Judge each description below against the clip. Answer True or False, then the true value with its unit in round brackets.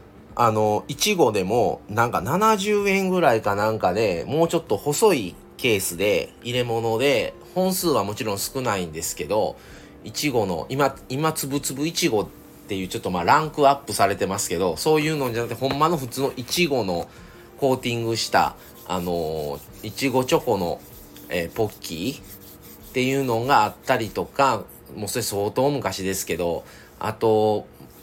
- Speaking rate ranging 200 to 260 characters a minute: False (330 characters per minute)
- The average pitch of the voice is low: True (125 Hz)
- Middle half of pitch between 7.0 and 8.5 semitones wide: False (6.5 semitones)